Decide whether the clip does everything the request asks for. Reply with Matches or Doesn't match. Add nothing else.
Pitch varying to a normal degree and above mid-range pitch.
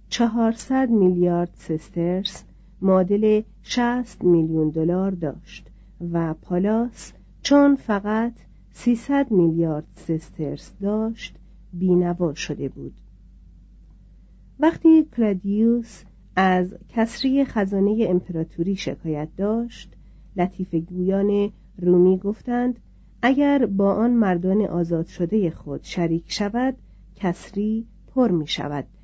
Matches